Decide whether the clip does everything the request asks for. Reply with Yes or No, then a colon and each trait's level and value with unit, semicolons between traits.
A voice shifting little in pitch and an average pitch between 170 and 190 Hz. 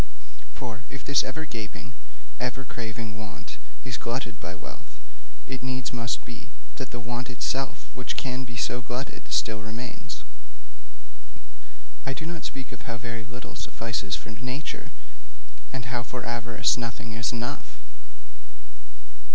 No: narrow, 1.9 semitones; low, 120 Hz